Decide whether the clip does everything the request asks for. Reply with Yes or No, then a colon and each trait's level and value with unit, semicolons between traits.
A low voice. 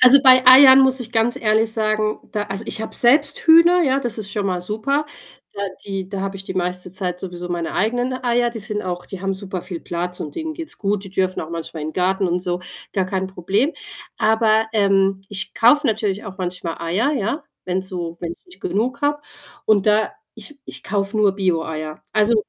No: high, 205 Hz